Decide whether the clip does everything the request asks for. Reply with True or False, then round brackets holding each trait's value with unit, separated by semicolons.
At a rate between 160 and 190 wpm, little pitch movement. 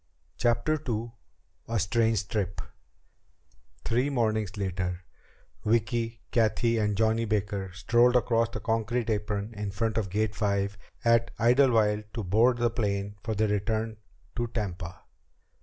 False (135 wpm; 2.2 semitones)